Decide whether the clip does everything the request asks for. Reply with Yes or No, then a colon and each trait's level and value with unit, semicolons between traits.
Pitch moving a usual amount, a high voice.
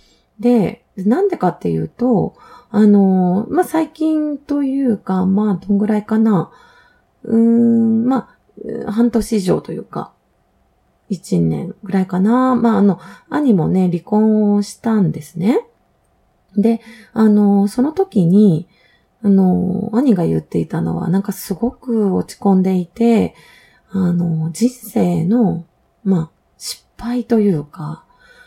Yes: average, 4.1 semitones; high, 210 Hz